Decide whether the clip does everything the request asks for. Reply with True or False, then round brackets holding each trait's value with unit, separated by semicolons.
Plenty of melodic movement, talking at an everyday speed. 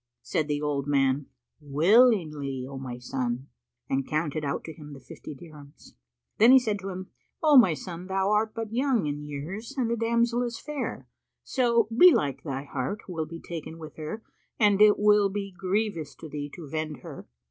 True (6.8 semitones; 185 wpm)